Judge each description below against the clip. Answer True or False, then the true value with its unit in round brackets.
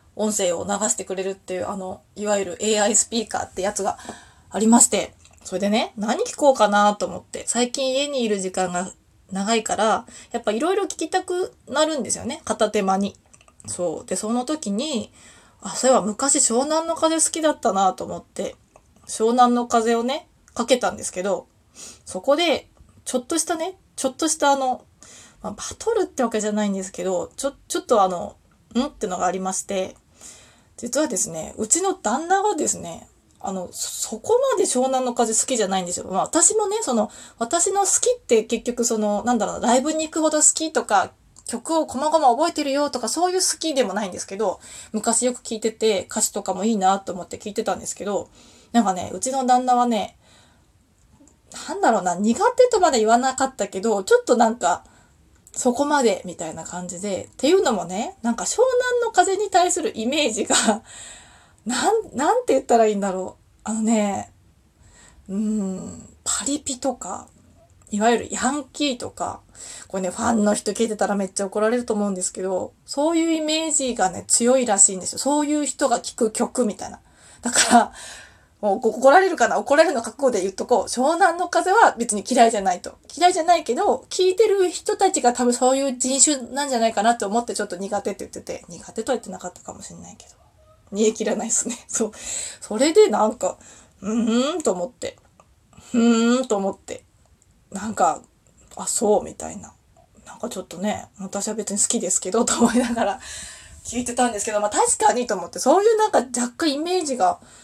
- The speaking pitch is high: True (235 Hz)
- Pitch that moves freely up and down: True (6.3 semitones)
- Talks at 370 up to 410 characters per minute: True (375 characters per minute)